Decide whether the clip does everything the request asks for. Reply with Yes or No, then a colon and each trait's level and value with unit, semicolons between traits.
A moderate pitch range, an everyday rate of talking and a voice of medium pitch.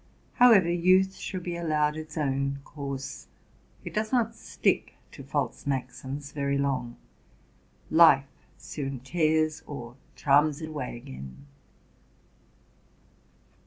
No: average, 3.6 semitones; slow, 110 wpm; medium, 145 Hz